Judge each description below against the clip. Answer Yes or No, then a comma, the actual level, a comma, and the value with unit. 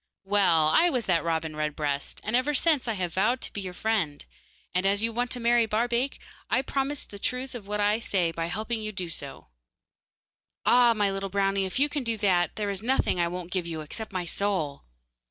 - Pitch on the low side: No, high, 200 Hz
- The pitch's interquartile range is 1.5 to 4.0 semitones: No, average, 5.1 semitones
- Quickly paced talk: Yes, fast, 225 wpm